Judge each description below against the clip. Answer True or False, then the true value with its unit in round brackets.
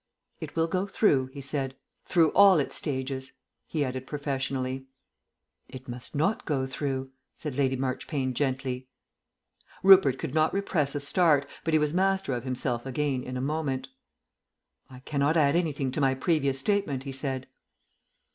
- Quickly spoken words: False (155 wpm)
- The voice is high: False (140 Hz)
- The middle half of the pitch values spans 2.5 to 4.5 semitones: True (2.9 semitones)